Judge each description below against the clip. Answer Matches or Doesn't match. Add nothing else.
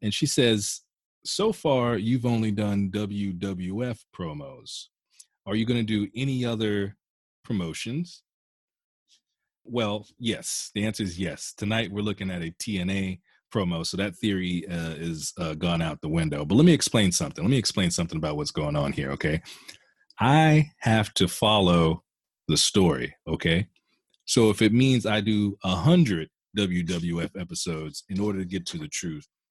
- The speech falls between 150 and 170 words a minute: Matches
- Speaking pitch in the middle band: Doesn't match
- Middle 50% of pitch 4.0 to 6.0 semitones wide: Matches